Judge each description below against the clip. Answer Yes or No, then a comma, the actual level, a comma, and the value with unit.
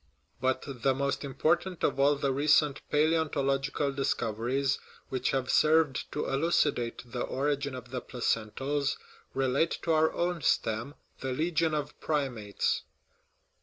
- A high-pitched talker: No, medium, 140 Hz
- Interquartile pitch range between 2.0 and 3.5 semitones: Yes, average, 2.7 semitones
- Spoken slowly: Yes, slow, 130 wpm